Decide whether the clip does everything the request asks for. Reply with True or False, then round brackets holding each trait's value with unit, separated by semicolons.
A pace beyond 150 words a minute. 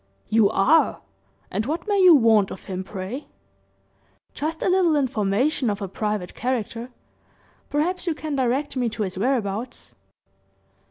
False (145 wpm)